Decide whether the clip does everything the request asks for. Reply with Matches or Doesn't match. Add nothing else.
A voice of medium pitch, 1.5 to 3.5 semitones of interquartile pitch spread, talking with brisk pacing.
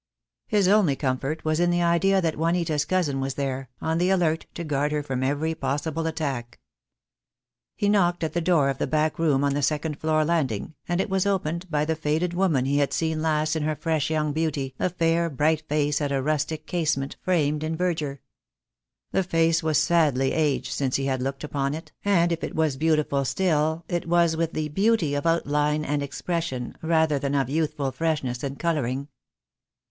Doesn't match